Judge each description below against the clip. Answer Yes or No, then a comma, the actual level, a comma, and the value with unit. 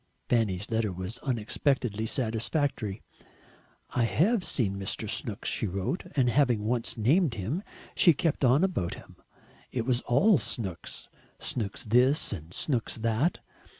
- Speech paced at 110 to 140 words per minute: Yes, slow, 135 wpm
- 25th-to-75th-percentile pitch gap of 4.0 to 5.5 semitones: Yes, average, 4.9 semitones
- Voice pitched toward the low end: Yes, low, 120 Hz